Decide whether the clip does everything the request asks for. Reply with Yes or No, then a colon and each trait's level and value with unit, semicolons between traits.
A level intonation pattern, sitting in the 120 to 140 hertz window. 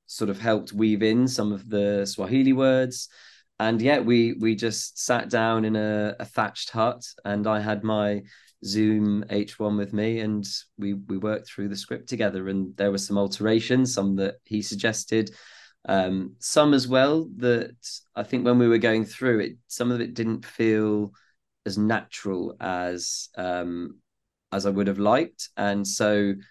No: narrow, 2.1 semitones; low, 105 Hz